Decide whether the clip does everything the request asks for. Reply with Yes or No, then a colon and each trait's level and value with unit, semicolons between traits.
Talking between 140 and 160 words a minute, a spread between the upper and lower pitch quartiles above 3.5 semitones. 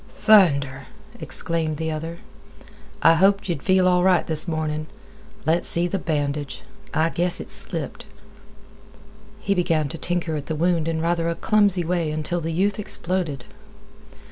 No: average, 145 wpm; narrow, 2.6 semitones